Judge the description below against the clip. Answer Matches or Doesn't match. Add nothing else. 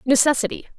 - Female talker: Matches